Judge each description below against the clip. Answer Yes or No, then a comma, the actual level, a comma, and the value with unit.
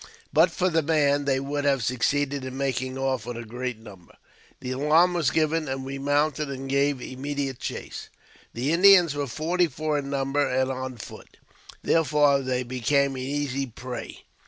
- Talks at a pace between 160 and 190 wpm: Yes, average, 175 wpm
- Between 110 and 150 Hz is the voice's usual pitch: Yes, medium, 140 Hz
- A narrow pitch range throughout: Yes, narrow, 2.3 semitones